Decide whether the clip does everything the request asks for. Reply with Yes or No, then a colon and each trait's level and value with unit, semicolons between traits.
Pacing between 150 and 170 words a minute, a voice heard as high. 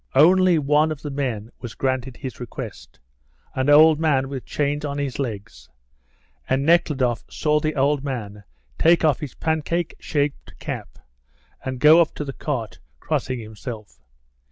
No: average, 155 wpm; medium, 140 Hz